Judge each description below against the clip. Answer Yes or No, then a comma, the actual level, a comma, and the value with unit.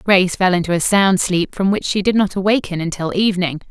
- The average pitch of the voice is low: No, medium, 185 Hz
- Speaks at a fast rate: Yes, fast, 225 wpm